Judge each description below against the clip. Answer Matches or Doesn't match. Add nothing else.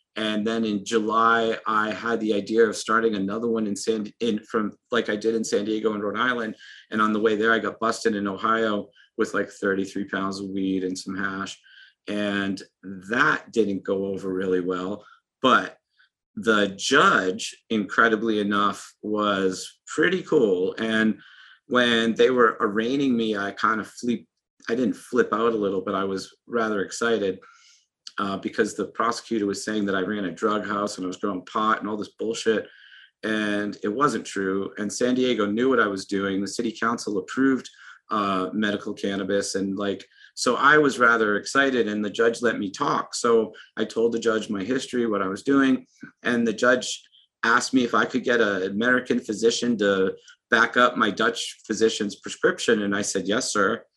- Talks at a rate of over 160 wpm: Matches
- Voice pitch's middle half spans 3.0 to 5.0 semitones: Doesn't match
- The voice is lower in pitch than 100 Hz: Doesn't match